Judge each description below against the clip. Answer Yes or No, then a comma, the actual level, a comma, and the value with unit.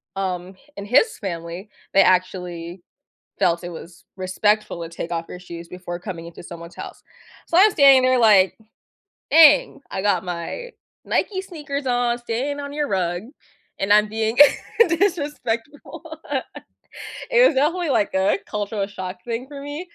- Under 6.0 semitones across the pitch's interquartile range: No, wide, 7.8 semitones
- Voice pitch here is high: Yes, high, 210 Hz